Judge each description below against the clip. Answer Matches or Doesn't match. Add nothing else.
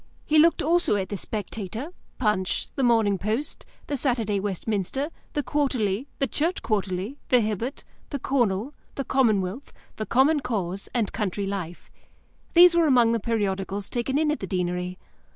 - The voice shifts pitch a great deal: Matches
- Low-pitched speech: Doesn't match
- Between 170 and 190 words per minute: Doesn't match